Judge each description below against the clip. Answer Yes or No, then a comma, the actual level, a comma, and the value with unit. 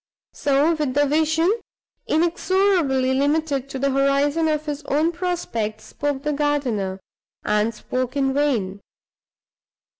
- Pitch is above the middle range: Yes, very high, 285 Hz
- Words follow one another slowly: Yes, slow, 115 wpm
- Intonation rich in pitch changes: No, average, 3.2 semitones